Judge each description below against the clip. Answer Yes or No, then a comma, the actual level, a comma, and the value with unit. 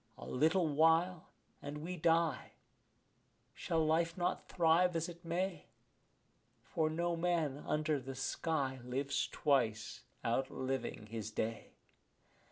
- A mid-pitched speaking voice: Yes, medium, 155 Hz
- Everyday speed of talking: No, slow, 115 wpm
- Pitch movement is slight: No, average, 4.1 semitones